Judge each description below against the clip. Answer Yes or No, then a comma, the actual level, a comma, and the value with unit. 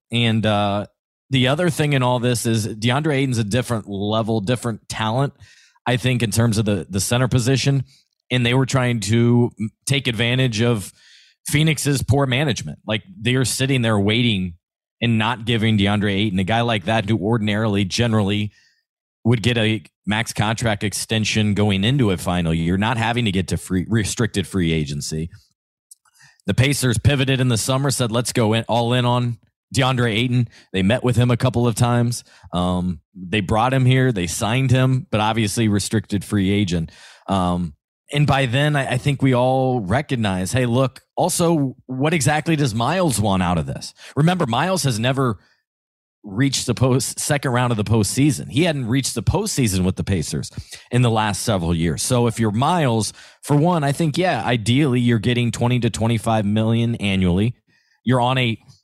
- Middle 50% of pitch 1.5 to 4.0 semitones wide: Yes, average, 3.5 semitones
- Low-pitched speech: Yes, low, 120 Hz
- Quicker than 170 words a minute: Yes, average, 180 wpm